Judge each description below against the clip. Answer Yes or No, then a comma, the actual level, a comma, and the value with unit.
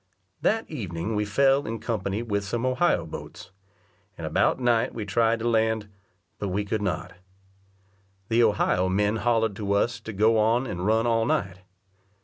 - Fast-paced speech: No, average, 165 wpm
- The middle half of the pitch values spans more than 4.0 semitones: No, narrow, 2.6 semitones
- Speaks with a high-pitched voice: No, low, 110 Hz